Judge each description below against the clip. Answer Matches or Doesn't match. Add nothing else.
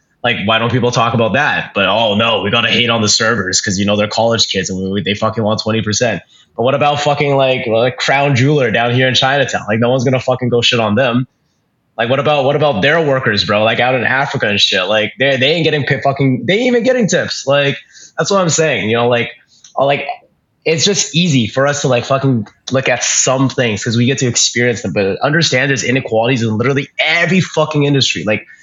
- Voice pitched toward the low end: Matches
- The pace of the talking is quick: Matches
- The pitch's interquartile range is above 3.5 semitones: Matches